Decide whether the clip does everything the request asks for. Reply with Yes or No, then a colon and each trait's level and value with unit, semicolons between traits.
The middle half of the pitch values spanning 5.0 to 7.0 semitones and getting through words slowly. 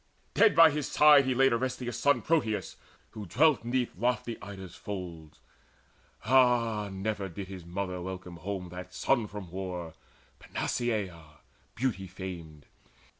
Yes: average, 5.3 semitones; slow, 130 wpm